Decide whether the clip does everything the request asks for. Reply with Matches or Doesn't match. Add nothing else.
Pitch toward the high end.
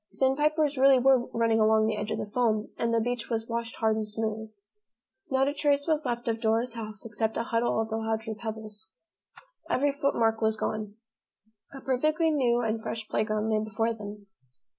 Matches